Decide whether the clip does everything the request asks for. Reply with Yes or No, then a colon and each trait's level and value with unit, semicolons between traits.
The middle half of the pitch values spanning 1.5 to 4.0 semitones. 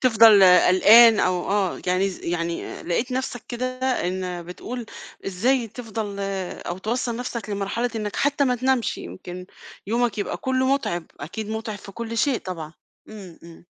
No: average, 5.0 semitones